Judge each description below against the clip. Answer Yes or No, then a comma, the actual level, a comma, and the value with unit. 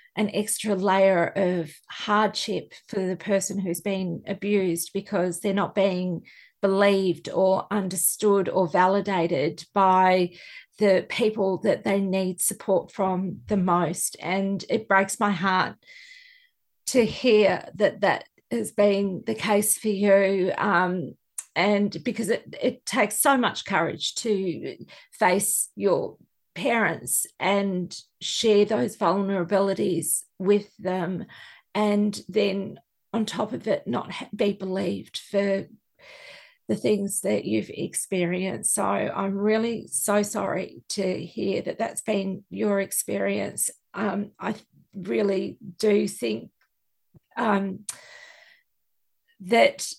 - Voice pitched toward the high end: Yes, high, 195 Hz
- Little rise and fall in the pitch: Yes, narrow, 1.9 semitones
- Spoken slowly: Yes, slow, 120 wpm